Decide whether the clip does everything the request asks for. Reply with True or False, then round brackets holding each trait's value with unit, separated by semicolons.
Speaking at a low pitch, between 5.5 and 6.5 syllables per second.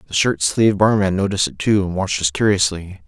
True (95 Hz; 6.3 syllables/s)